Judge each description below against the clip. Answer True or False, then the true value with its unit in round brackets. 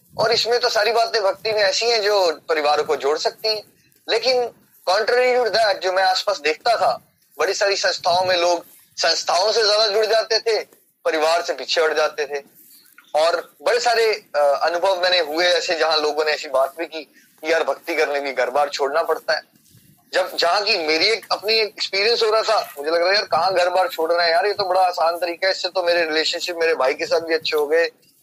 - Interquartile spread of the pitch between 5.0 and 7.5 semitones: True (5.3 semitones)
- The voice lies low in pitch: False (185 Hz)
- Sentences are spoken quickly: True (215 wpm)